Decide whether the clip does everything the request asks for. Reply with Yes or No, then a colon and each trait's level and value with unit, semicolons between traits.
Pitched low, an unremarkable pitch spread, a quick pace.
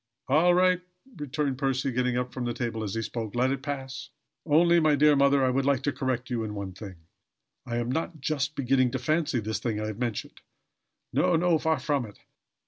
Yes: low, 130 Hz; average, 3.7 semitones; fast, 215 wpm